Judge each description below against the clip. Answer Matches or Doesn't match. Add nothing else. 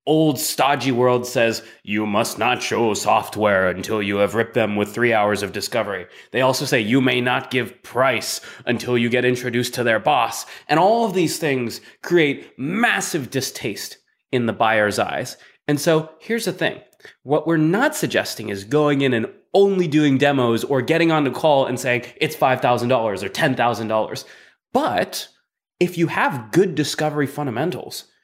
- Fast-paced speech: Doesn't match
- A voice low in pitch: Matches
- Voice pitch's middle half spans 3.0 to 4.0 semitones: Doesn't match